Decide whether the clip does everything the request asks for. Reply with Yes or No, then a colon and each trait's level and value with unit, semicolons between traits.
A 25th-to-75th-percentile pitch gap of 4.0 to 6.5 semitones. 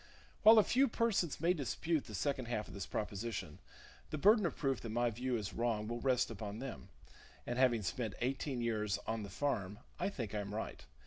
Yes: average, 4.9 semitones